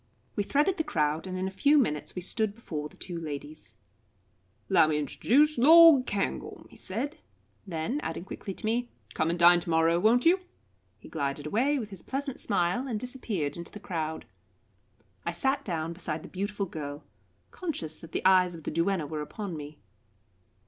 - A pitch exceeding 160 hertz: Yes, medium, 185 Hz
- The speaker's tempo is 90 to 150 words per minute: No, average, 175 wpm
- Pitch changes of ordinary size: No, wide, 7.2 semitones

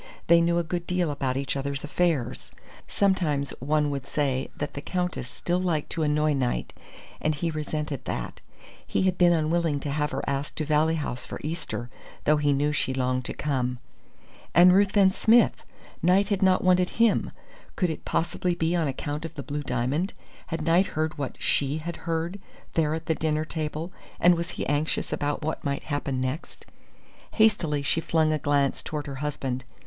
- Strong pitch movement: No, average, 3.3 semitones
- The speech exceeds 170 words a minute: Yes, average, 185 wpm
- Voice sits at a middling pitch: Yes, medium, 155 Hz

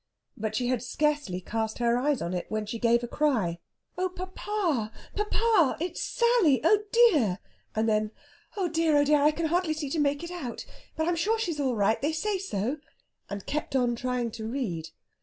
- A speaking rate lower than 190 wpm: No, average, 195 wpm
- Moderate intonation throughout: No, wide, 7.0 semitones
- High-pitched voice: Yes, very high, 285 Hz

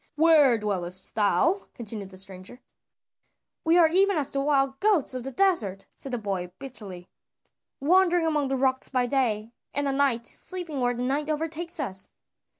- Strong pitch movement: Yes, wide, 6.8 semitones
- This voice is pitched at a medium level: No, very high, 270 Hz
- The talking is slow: No, average, 165 wpm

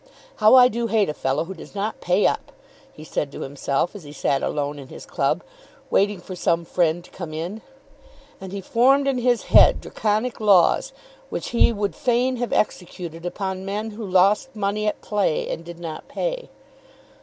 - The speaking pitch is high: Yes, high, 195 Hz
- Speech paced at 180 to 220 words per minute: Yes, average, 190 wpm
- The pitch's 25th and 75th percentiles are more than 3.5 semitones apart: Yes, average, 4.7 semitones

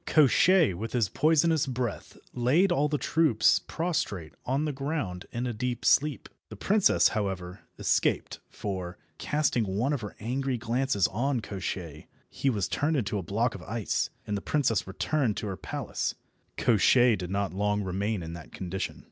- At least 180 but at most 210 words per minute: No, average, 165 wpm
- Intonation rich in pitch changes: Yes, wide, 6.0 semitones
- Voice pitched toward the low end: Yes, low, 115 Hz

